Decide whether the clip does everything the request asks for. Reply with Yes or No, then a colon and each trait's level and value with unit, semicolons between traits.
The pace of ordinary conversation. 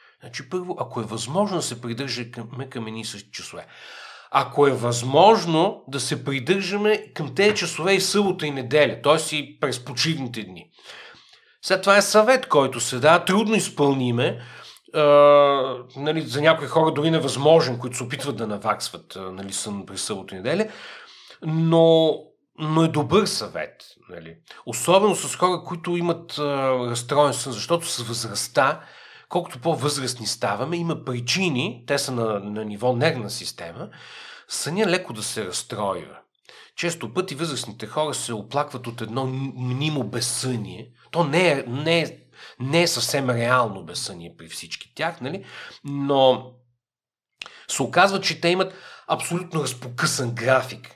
Yes: average, 145 wpm